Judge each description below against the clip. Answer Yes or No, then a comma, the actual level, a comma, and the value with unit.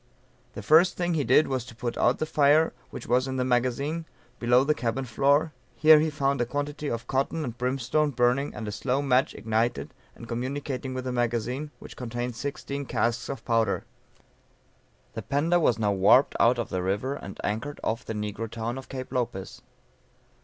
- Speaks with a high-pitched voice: No, low, 125 Hz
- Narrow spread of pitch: No, average, 3.4 semitones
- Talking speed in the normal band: Yes, average, 190 wpm